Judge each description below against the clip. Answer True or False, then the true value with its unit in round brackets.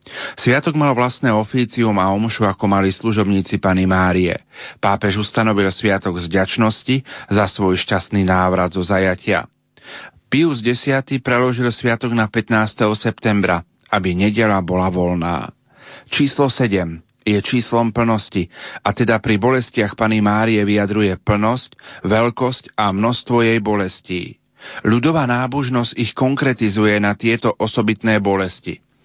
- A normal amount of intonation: True (3.6 semitones)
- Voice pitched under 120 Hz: True (110 Hz)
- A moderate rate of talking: True (120 wpm)